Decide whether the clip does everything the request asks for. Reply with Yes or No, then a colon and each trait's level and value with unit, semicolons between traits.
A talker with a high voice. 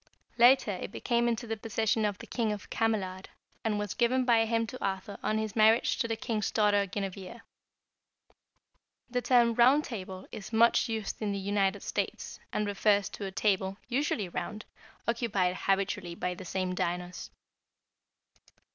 Yes: high, 210 Hz